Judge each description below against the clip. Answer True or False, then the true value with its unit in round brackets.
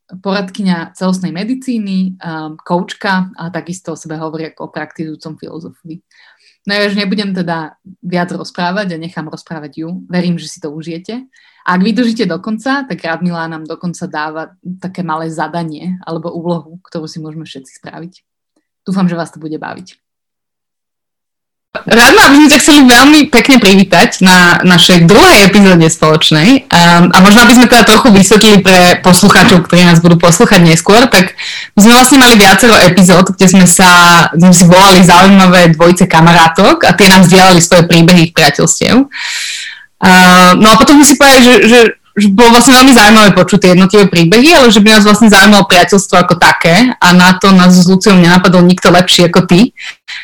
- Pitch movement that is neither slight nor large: True (3.4 semitones)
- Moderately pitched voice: True (180 Hz)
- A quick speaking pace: True (170 wpm)